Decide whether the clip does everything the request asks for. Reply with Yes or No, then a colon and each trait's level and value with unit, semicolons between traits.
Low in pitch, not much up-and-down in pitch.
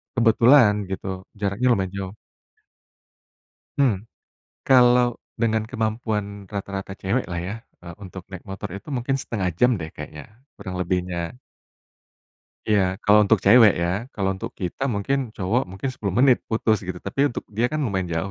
No: low, 105 Hz; average, 4.1 semitones